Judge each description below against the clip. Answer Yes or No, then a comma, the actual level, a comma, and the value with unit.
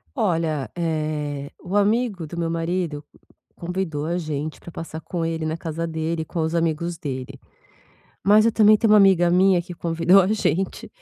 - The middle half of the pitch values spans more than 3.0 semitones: No, average, 2.7 semitones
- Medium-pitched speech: Yes, medium, 165 Hz